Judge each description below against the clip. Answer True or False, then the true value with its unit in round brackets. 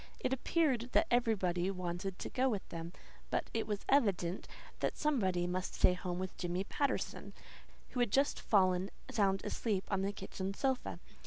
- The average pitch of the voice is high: True (195 Hz)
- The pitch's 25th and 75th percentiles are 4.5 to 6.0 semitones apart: True (4.9 semitones)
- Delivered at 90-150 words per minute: False (165 wpm)